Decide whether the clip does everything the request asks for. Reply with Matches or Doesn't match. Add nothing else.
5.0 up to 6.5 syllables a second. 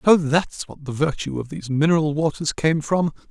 Matches